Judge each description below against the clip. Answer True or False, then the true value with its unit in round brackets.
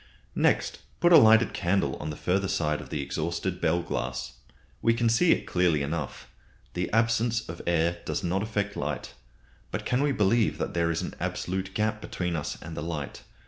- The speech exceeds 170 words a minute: True (190 wpm)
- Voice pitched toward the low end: True (90 Hz)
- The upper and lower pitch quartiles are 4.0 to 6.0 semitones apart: True (4.9 semitones)